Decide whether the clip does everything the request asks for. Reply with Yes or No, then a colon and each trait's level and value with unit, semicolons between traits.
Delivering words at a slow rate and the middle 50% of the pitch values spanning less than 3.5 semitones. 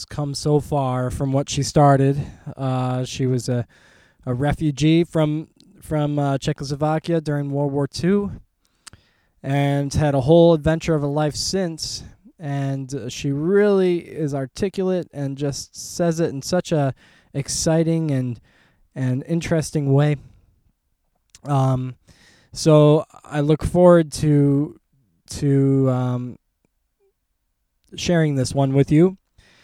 Yes: slow, 125 wpm; average, 2.9 semitones